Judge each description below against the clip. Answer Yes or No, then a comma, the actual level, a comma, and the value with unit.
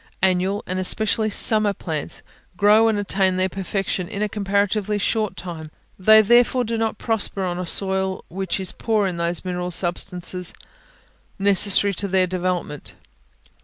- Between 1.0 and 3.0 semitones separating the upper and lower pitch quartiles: Yes, narrow, 2.4 semitones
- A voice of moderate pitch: No, high, 195 Hz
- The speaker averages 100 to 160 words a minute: Yes, average, 150 wpm